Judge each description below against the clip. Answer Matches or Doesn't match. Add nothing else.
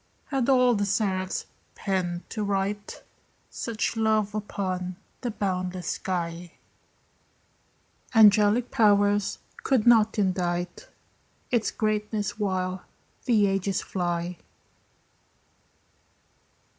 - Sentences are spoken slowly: Matches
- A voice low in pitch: Doesn't match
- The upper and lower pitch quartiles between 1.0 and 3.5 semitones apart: Matches